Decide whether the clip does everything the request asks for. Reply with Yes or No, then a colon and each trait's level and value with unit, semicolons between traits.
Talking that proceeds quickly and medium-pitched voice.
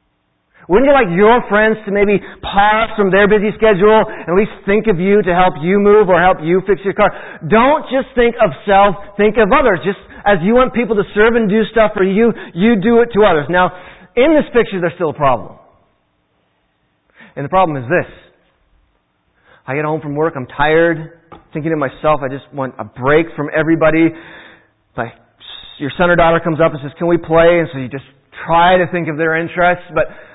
Yes: fast, 210 wpm; medium, 180 Hz